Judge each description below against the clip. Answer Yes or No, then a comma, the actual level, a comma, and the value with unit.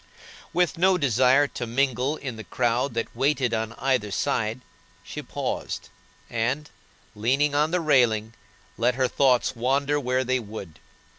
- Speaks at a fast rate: No, average, 145 wpm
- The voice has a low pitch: Yes, low, 130 Hz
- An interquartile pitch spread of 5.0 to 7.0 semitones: No, average, 3.5 semitones